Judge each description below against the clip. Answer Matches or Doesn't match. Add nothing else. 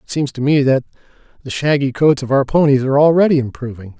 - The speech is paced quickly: Matches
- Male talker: Matches